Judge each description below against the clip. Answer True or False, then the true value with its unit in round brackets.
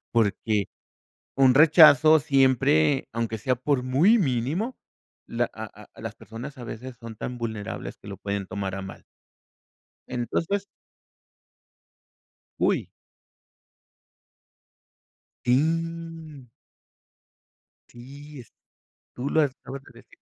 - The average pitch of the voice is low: True (130 Hz)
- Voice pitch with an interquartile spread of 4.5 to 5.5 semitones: True (4.8 semitones)